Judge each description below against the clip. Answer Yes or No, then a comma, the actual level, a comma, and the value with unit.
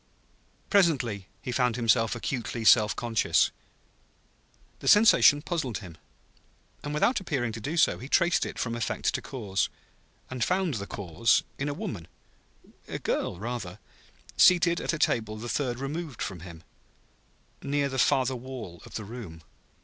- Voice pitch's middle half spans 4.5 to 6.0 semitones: Yes, average, 5.1 semitones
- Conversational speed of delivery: Yes, average, 150 wpm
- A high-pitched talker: No, low, 120 Hz